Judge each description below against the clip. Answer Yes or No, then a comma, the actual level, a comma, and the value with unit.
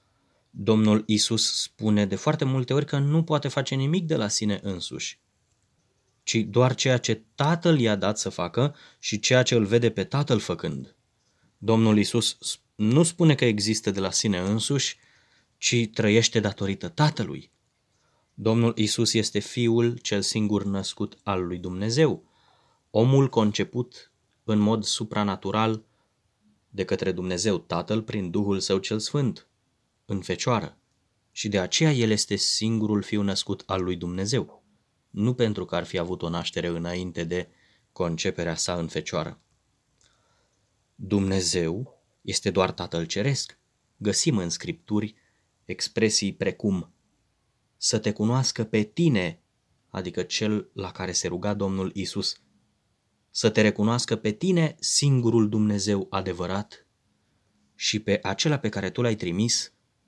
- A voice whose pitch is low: Yes, low, 105 Hz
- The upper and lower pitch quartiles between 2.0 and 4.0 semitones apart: Yes, average, 3.3 semitones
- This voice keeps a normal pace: Yes, average, 135 wpm